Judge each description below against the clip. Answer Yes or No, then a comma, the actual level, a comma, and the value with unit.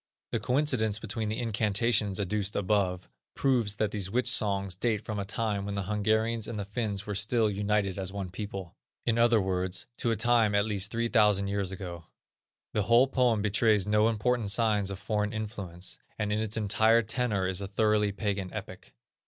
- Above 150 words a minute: Yes, average, 185 wpm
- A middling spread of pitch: No, narrow, 2.2 semitones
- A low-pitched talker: Yes, low, 105 Hz